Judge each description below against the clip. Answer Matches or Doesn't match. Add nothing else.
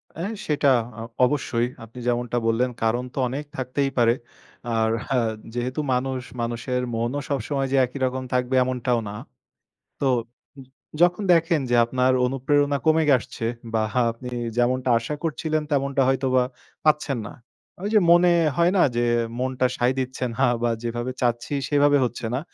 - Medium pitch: Doesn't match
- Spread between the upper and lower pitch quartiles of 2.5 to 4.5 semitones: Matches